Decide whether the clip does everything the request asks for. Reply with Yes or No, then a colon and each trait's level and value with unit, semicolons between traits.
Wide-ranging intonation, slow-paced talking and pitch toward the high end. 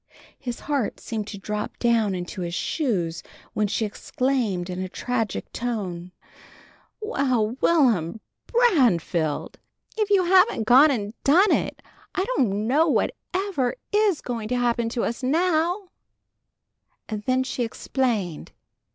Yes: wide, 6.4 semitones; slow, 130 wpm; high, 240 Hz